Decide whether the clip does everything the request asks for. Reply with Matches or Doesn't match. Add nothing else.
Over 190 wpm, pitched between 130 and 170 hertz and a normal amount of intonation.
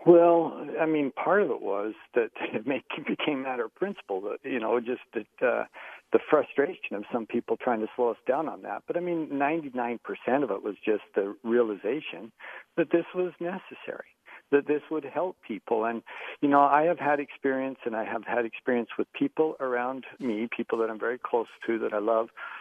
Doesn't match